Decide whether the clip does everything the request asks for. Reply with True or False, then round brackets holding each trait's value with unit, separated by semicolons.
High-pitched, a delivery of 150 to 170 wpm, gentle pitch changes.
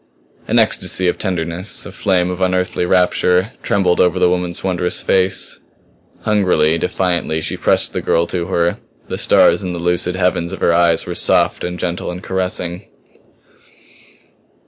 False (90 Hz; 155 wpm; 1.2 semitones)